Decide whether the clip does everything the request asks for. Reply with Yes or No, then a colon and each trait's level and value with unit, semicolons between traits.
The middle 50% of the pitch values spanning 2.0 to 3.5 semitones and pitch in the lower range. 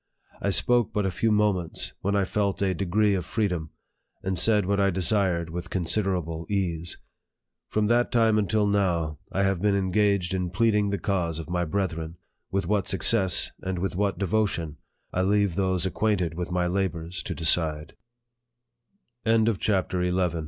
Yes: average, 2.8 semitones; very low, 95 Hz